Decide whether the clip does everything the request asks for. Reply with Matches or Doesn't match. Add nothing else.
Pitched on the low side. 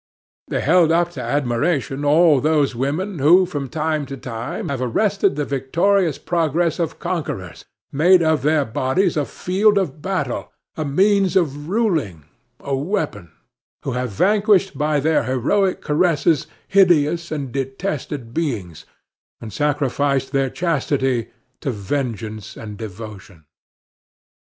Doesn't match